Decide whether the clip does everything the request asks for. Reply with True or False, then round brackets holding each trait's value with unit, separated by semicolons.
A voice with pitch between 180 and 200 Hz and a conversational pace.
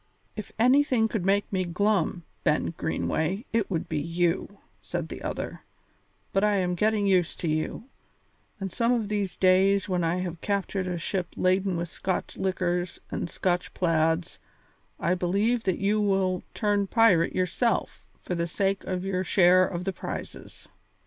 True (185 Hz; 160 wpm)